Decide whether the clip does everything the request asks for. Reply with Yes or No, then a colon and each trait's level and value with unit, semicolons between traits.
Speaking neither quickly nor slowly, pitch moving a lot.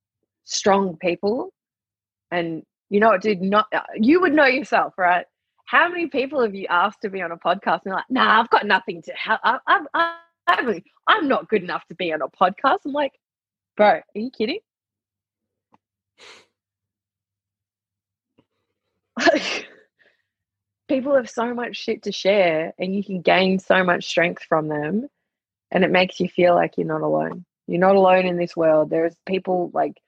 Yes: average, 170 wpm; wide, 7.3 semitones